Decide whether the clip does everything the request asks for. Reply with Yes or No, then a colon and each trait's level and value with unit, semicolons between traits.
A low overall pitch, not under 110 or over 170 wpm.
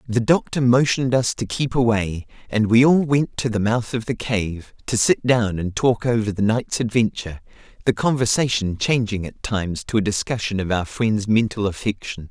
No: low, 110 Hz; average, 190 wpm